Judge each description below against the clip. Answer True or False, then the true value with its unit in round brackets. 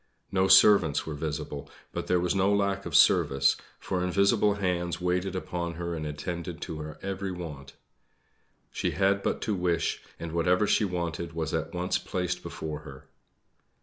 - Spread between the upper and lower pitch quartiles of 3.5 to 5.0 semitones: False (3.0 semitones)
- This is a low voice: True (90 Hz)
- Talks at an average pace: True (165 wpm)